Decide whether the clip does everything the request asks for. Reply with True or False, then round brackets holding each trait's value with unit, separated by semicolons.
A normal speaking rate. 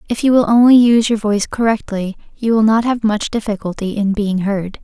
False (210 wpm)